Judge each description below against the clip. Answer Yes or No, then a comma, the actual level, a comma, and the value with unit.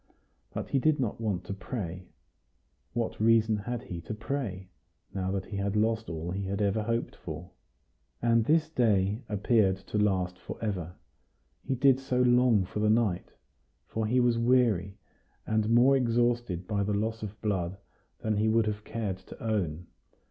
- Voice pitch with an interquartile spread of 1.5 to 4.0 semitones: Yes, average, 3.3 semitones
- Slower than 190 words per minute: Yes, average, 170 wpm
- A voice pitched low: Yes, low, 110 Hz